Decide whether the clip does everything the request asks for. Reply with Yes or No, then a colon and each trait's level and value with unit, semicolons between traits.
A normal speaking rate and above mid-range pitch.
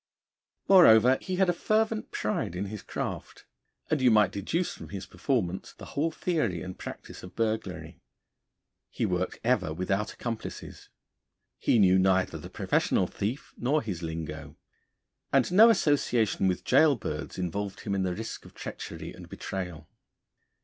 No: average, 150 wpm; low, 105 Hz